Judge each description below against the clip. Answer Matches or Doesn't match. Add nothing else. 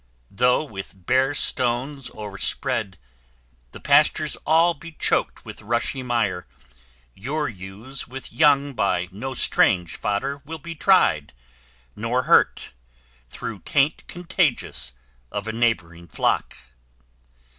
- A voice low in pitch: Matches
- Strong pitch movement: Matches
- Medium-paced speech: Doesn't match